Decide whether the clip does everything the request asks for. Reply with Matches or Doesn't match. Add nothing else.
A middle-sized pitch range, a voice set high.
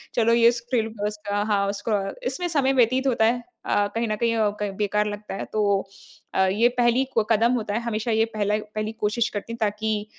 Doesn't match